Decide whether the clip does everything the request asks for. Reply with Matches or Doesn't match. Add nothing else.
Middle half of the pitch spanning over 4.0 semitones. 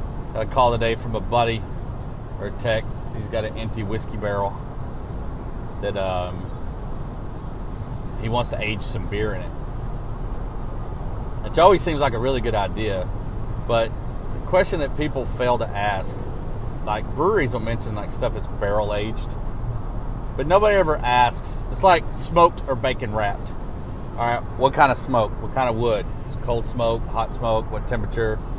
Doesn't match